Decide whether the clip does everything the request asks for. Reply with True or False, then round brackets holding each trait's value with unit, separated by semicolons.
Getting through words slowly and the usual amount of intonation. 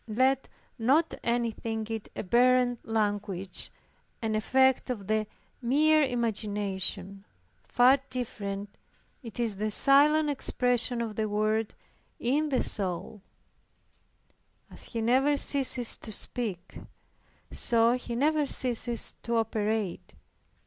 True (115 wpm; 3.2 semitones)